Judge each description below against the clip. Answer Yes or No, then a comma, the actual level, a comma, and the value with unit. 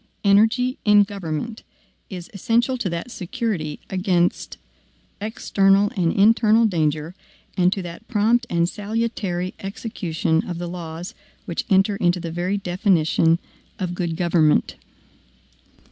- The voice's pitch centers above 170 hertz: Yes, medium, 185 Hz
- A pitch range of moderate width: Yes, average, 3.6 semitones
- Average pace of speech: No, slow, 120 wpm